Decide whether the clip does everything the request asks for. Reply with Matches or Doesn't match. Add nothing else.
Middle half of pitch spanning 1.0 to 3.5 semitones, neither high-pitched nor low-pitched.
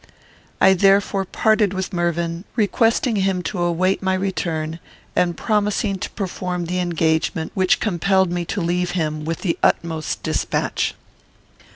Matches